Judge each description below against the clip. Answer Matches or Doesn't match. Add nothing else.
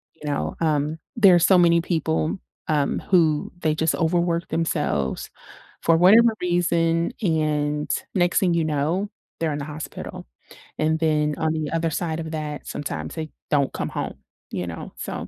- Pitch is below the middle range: Doesn't match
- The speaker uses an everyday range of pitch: Doesn't match